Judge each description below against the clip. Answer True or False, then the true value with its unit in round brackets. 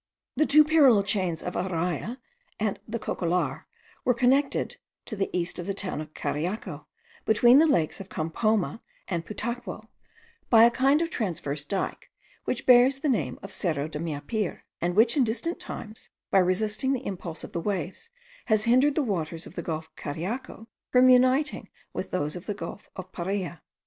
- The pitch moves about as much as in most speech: False (6.4 semitones)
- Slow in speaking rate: False (175 wpm)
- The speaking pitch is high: True (205 Hz)